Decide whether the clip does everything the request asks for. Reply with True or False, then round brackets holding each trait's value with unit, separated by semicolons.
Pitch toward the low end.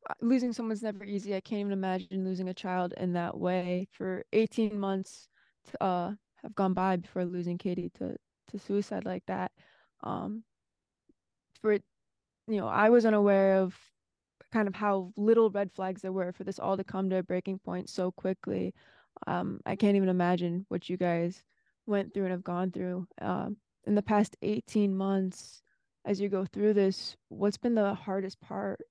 False (195 Hz)